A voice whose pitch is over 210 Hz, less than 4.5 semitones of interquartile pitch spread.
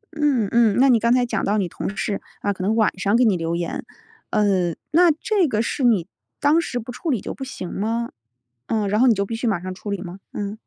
Yes: high, 220 Hz; average, 3.9 semitones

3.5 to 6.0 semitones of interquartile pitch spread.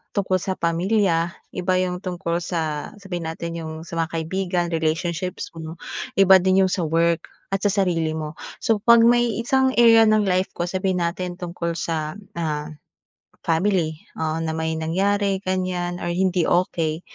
No: average, 2.7 semitones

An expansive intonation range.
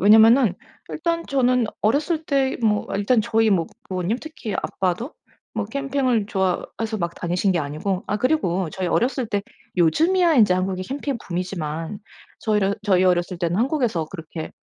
Yes: wide, 5.9 semitones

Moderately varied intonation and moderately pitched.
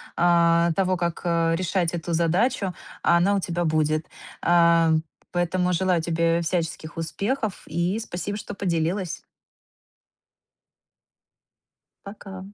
No: narrow, 1.9 semitones; medium, 170 Hz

